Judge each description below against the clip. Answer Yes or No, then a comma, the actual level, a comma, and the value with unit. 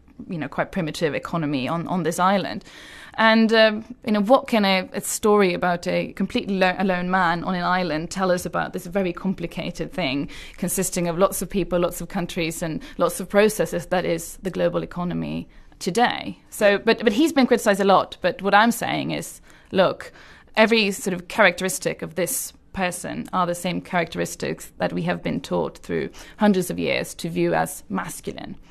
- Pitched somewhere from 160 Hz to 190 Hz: Yes, medium, 185 Hz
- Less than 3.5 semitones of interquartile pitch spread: Yes, average, 2.8 semitones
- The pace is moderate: Yes, average, 190 wpm